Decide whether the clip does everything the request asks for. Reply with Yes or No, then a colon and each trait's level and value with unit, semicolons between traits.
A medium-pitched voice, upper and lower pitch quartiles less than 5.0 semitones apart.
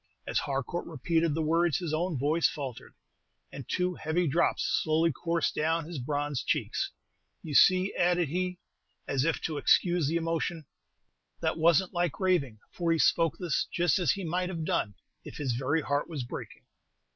Yes: medium, 165 Hz; average, 3.1 semitones